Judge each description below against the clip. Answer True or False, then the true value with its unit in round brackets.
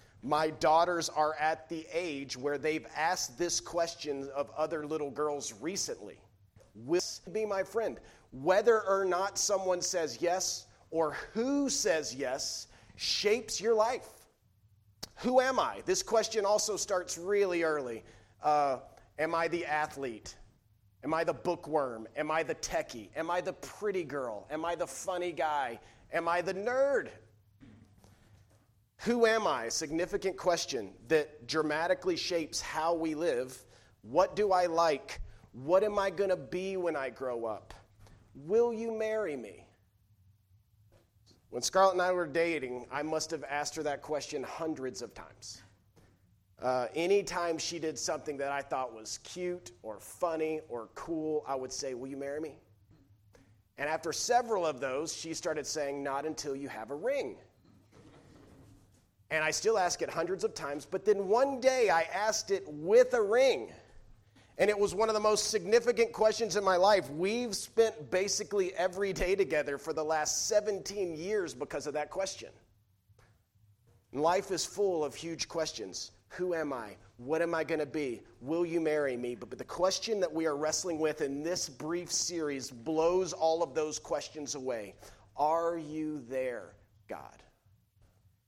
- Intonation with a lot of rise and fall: True (7.0 semitones)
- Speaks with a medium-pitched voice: True (155 Hz)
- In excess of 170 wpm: False (160 wpm)